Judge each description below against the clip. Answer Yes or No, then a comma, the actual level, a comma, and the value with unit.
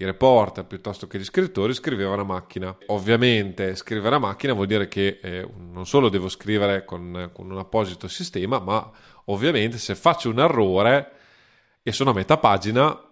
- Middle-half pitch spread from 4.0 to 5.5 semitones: No, average, 3.0 semitones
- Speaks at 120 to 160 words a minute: No, fast, 170 wpm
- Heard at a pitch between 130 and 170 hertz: No, low, 100 Hz